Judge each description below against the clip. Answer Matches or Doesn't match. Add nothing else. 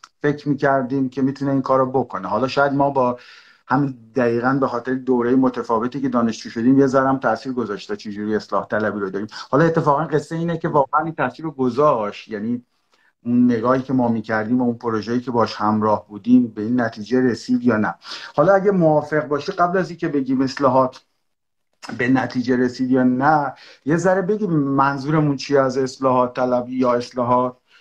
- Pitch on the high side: Doesn't match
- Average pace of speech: Doesn't match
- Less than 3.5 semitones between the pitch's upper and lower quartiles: Matches